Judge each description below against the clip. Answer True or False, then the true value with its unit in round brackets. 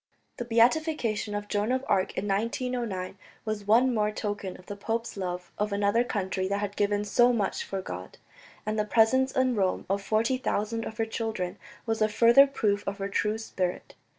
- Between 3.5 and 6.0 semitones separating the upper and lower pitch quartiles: False (2.6 semitones)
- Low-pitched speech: False (210 Hz)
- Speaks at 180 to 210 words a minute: True (195 wpm)